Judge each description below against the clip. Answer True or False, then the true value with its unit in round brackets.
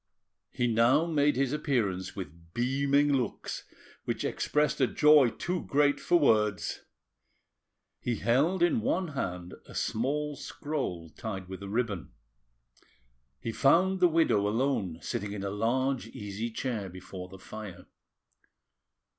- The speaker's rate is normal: False (130 wpm)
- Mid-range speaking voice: False (120 Hz)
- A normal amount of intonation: False (6.5 semitones)